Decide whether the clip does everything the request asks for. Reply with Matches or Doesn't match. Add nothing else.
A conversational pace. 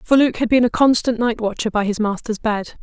Doesn't match